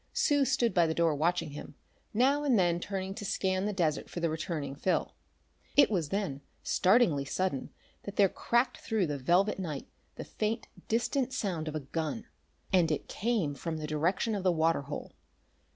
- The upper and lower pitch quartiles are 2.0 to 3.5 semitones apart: No, wide, 5.4 semitones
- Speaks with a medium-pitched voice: Yes, medium, 180 Hz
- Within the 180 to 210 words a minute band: Yes, average, 185 wpm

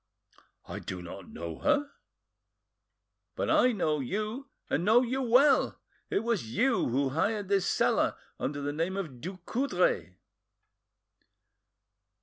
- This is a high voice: Yes, high, 200 Hz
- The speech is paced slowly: Yes, slow, 125 wpm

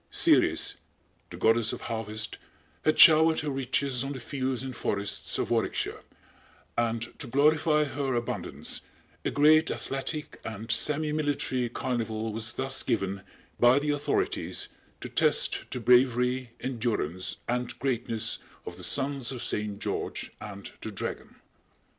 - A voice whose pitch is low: Yes, low, 125 Hz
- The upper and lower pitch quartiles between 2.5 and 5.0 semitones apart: Yes, average, 3.8 semitones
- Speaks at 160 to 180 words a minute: No, slow, 135 wpm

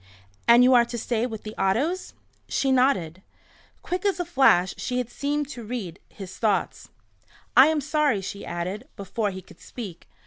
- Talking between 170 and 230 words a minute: Yes, average, 175 wpm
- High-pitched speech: Yes, high, 235 Hz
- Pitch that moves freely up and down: Yes, wide, 6.0 semitones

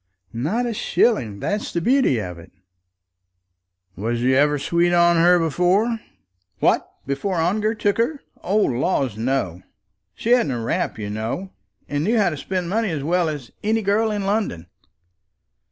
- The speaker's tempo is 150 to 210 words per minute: Yes, average, 160 wpm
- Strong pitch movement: Yes, wide, 8.0 semitones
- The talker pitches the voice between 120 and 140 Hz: No, medium, 175 Hz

